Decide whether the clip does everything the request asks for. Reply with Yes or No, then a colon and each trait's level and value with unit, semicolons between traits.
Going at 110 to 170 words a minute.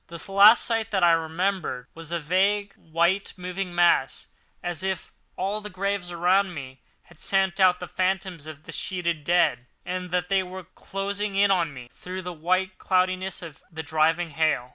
No: average, 180 wpm